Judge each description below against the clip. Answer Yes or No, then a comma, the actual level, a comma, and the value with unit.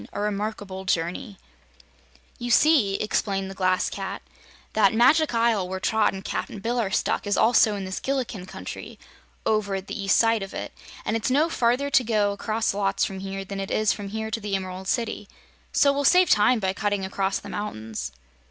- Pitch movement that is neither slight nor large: Yes, average, 3.0 semitones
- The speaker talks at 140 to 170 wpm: No, average, 195 wpm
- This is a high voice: Yes, high, 205 Hz